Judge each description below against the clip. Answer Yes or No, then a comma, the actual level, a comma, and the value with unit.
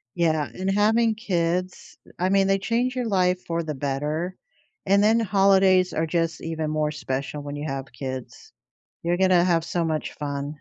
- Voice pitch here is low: No, medium, 175 Hz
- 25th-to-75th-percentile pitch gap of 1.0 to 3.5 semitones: No, average, 4.2 semitones